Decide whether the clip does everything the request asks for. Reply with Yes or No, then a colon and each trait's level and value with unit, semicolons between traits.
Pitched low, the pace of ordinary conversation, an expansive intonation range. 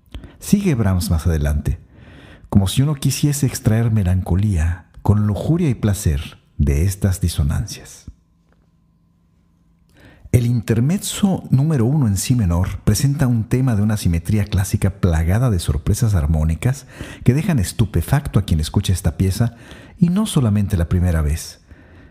Yes: low, 100 Hz; average, 135 wpm; wide, 6.0 semitones